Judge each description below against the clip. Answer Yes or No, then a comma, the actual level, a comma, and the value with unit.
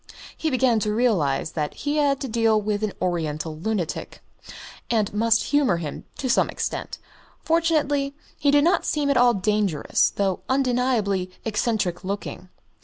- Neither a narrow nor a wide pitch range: No, wide, 6.0 semitones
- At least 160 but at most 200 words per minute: No, average, 150 wpm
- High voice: Yes, high, 220 Hz